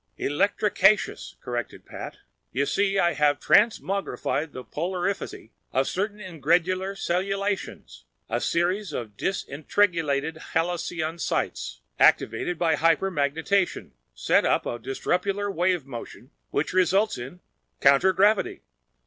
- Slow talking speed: Yes, slow, 100 wpm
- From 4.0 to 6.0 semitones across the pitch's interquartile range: Yes, average, 4.8 semitones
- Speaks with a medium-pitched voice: Yes, medium, 175 Hz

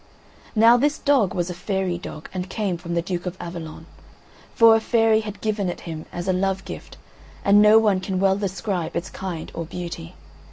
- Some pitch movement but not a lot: Yes, average, 3.5 semitones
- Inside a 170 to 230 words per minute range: Yes, average, 200 wpm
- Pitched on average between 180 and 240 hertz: Yes, high, 190 Hz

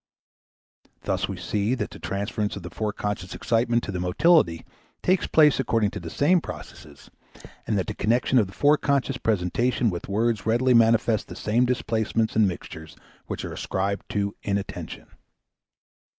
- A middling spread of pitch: Yes, average, 3.8 semitones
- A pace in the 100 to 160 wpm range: Yes, average, 155 wpm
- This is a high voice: No, low, 110 Hz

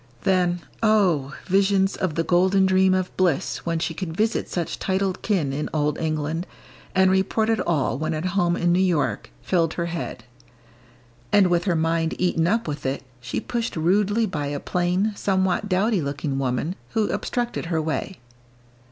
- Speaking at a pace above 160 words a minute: Yes, average, 170 wpm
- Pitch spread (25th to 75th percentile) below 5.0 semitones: Yes, average, 3.3 semitones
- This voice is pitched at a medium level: Yes, medium, 175 Hz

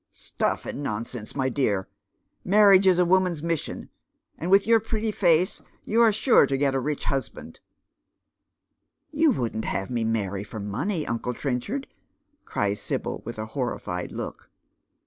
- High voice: No, medium, 145 Hz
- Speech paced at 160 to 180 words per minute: Yes, average, 170 wpm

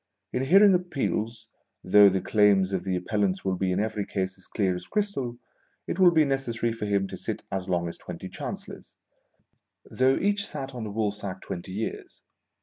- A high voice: No, low, 105 Hz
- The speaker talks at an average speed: Yes, average, 185 wpm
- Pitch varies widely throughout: Yes, wide, 5.8 semitones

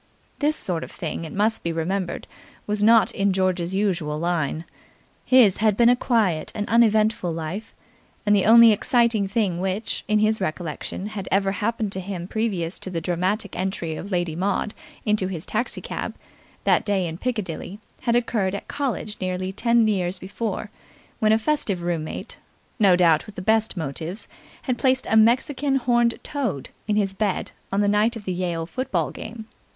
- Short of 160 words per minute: No, average, 175 wpm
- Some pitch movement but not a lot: Yes, average, 3.8 semitones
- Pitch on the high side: Yes, high, 200 Hz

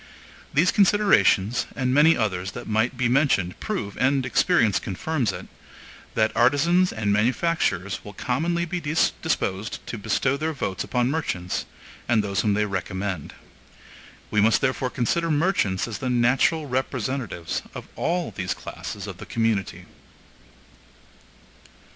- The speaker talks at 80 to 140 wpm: Yes, slow, 135 wpm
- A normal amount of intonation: No, wide, 6.9 semitones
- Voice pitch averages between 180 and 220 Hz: No, low, 120 Hz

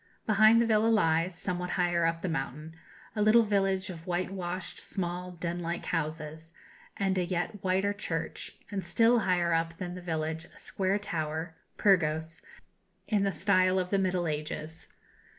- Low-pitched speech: No, medium, 180 Hz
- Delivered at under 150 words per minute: No, average, 165 wpm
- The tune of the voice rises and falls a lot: No, average, 2.9 semitones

